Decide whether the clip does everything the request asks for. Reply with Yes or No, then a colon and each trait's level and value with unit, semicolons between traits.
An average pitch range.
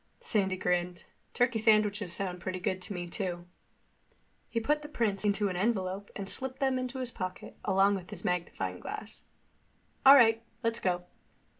Yes: average, 4.0 semitones